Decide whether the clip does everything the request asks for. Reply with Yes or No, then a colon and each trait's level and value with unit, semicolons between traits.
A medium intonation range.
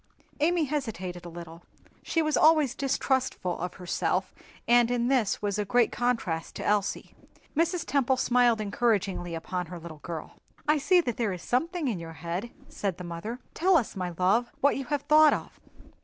No: wide, 7.3 semitones